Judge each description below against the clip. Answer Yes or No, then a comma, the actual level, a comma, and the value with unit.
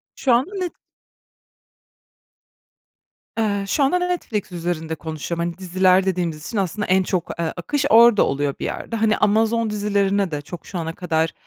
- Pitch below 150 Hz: No, high, 190 Hz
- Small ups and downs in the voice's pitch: No, average, 4.7 semitones